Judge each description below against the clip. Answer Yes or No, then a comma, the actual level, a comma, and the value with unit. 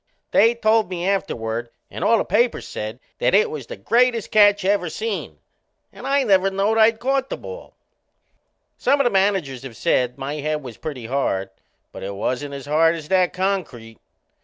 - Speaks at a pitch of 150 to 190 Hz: Yes, medium, 185 Hz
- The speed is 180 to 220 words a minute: Yes, average, 185 wpm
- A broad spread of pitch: Yes, wide, 8.3 semitones